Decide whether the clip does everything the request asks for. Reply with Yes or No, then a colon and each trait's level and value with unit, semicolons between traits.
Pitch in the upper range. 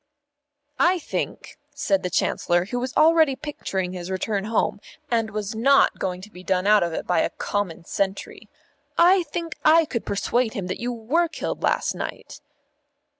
Yes: high, 220 Hz